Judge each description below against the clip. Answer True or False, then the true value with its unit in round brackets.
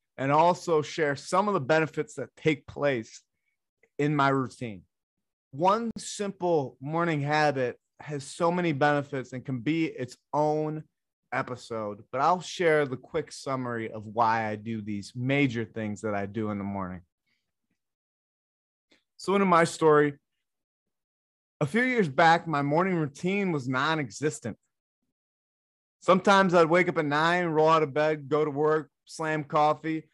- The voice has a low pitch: False (150 Hz)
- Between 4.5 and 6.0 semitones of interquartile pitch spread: True (4.9 semitones)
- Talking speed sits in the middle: True (150 wpm)